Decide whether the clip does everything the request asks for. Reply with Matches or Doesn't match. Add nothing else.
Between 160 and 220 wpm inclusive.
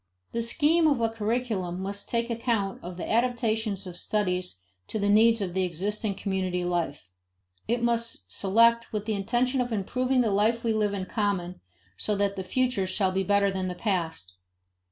Matches